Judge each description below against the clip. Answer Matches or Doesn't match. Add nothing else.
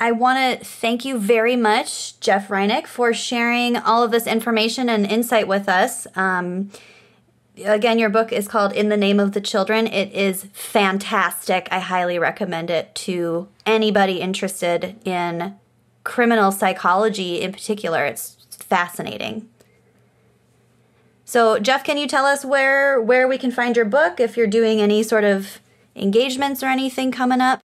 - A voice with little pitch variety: Doesn't match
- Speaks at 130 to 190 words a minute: Matches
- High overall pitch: Matches